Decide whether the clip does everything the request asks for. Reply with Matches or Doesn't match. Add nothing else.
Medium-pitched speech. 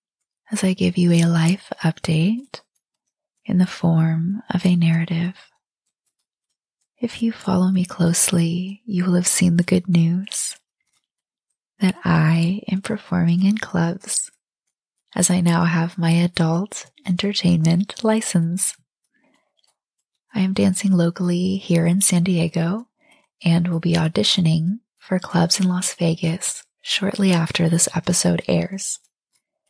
Matches